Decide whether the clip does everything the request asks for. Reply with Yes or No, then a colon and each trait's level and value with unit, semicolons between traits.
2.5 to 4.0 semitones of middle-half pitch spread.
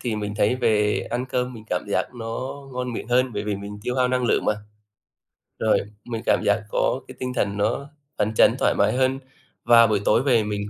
Yes: average, 3.2 semitones